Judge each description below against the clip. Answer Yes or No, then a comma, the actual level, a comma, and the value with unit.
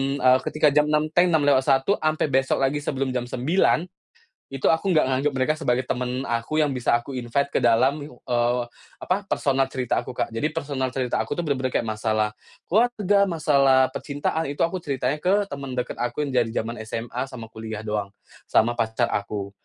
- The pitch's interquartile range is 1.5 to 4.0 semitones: Yes, average, 3.7 semitones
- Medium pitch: No, low, 130 Hz